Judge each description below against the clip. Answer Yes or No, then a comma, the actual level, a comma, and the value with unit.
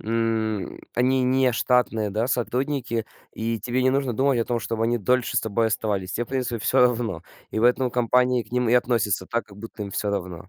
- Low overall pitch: Yes, low, 115 Hz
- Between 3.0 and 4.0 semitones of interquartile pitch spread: No, narrow, 2.4 semitones